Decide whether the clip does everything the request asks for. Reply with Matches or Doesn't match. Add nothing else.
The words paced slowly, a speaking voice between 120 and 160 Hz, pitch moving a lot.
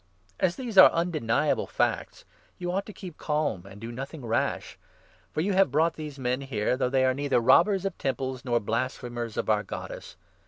Doesn't match